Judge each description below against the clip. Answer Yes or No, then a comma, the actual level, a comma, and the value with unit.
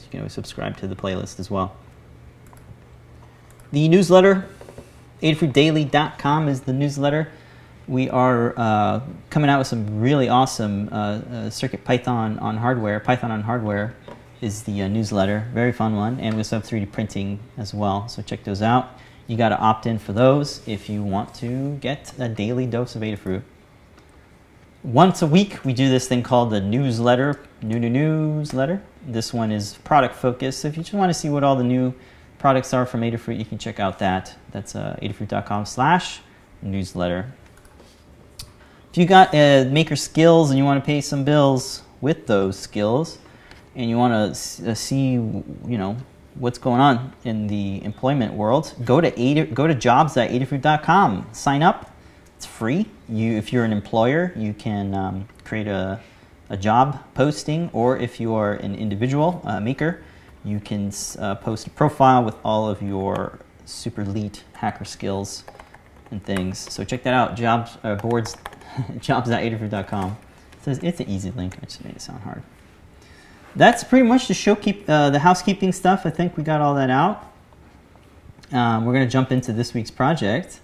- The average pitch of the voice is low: Yes, low, 120 Hz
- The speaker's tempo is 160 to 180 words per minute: Yes, average, 170 wpm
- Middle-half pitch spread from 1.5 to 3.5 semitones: No, average, 5.0 semitones